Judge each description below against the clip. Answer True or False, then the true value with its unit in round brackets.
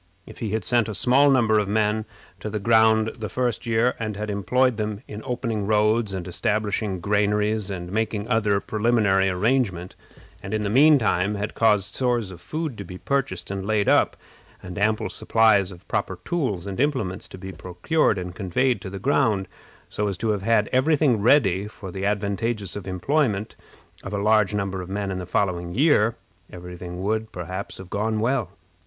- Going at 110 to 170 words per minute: False (185 wpm)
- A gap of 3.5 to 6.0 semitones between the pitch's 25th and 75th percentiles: False (2.9 semitones)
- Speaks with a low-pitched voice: True (105 Hz)